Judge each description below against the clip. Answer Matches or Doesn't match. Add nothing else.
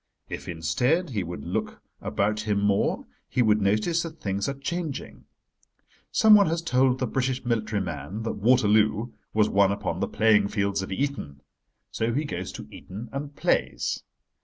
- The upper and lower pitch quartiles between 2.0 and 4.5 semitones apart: Doesn't match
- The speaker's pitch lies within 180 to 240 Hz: Doesn't match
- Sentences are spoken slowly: Doesn't match